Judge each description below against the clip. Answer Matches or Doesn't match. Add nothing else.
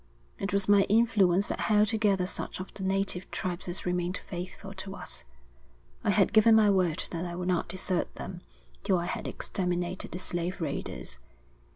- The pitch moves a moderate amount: Doesn't match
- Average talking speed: Matches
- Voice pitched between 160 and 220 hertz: Matches